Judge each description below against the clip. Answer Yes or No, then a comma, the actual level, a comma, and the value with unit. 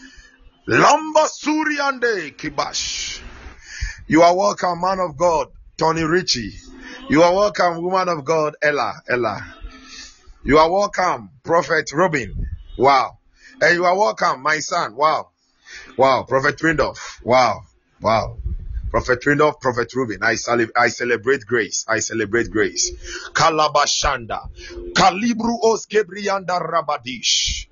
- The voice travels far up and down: Yes, wide, 7.4 semitones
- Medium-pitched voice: Yes, medium, 165 Hz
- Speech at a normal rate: No, slow, 115 wpm